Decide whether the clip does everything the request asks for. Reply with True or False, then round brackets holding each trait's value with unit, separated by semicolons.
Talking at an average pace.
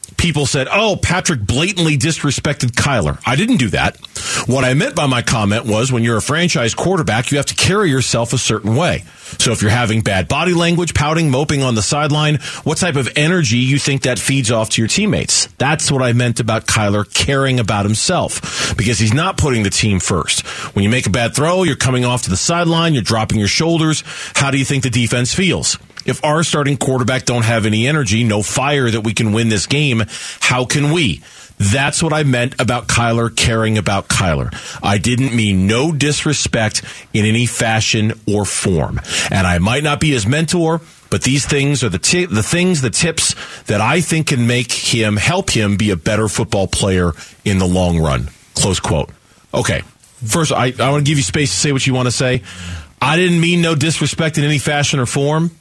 False (210 wpm)